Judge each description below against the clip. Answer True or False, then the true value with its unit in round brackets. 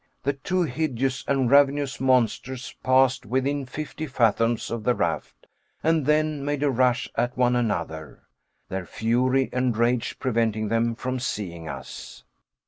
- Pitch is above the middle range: False (125 Hz)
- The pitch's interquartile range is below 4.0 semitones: True (2.9 semitones)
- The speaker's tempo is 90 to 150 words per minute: True (140 wpm)